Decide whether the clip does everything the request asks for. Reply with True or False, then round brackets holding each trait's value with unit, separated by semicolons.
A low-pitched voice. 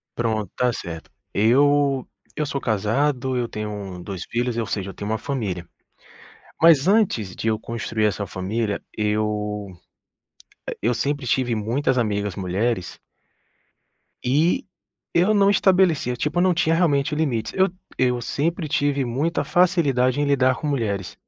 True (125 Hz)